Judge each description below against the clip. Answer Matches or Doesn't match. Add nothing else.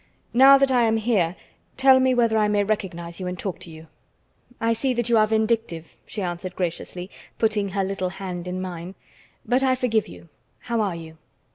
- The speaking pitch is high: Matches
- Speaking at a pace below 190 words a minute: Doesn't match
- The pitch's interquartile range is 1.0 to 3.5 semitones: Doesn't match